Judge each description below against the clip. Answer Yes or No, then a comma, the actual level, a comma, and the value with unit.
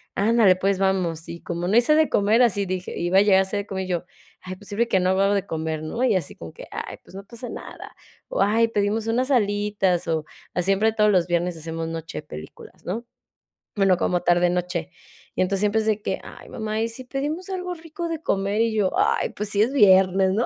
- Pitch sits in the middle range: No, high, 200 Hz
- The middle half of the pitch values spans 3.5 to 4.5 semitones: Yes, average, 3.8 semitones